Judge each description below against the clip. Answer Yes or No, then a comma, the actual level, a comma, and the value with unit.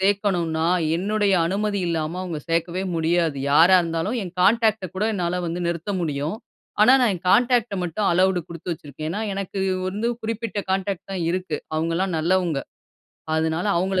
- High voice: No, medium, 180 Hz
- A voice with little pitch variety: No, average, 3.3 semitones